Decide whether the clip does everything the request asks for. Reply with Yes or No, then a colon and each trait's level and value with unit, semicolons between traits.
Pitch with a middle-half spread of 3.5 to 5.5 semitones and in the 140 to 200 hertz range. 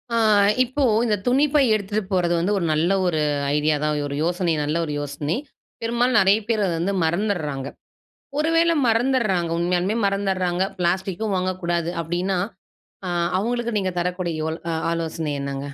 Yes: average, 4.3 semitones; medium, 185 Hz